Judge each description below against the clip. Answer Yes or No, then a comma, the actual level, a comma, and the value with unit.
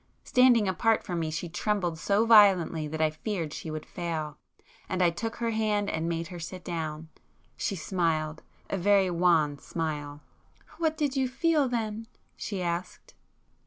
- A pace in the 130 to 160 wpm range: Yes, average, 155 wpm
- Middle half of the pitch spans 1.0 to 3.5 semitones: No, average, 5.1 semitones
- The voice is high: No, medium, 180 Hz